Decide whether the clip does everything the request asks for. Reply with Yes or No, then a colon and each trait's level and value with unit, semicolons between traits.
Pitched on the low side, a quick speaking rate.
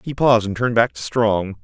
Yes: low, 110 Hz; fast, 260 wpm